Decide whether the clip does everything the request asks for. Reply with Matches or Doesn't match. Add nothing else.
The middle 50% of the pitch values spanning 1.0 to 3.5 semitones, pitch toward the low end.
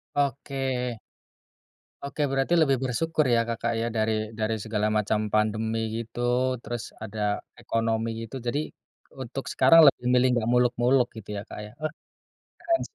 Matches